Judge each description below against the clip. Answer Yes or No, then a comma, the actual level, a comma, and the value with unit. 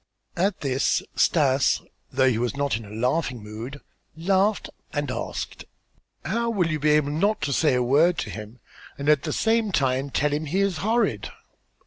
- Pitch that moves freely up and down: Yes, wide, 5.9 semitones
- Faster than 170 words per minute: Yes, average, 180 wpm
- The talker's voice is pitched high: No, medium, 145 Hz